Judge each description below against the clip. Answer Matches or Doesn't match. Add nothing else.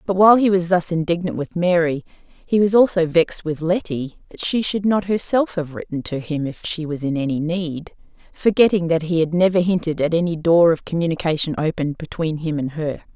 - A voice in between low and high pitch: Matches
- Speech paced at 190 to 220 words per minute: Matches